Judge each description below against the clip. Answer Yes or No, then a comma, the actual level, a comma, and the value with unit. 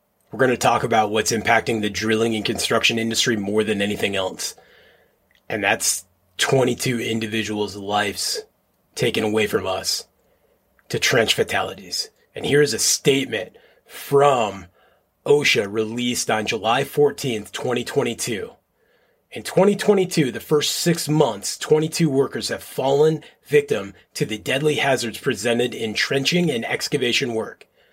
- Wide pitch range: Yes, wide, 7.4 semitones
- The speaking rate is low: Yes, slow, 130 wpm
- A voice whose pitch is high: No, low, 135 Hz